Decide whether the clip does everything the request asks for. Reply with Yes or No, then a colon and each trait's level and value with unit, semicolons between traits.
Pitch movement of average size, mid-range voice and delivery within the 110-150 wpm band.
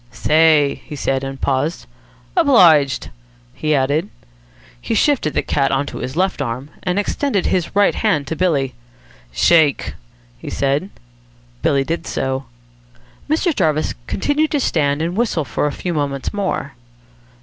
Yes: average, 4.9 semitones; medium, 150 Hz; average, 145 wpm